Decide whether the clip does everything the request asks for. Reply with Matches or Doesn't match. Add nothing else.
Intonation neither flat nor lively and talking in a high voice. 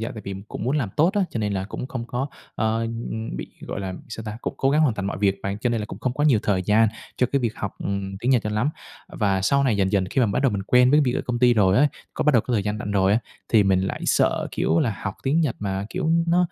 Doesn't match